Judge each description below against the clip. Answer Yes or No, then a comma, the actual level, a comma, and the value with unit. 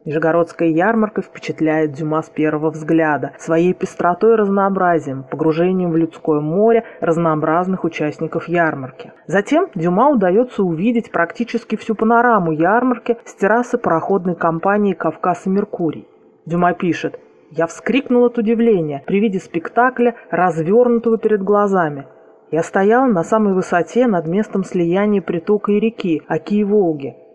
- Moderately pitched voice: Yes, medium, 180 Hz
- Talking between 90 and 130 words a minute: Yes, average, 125 wpm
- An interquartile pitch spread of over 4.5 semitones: Yes, average, 5.1 semitones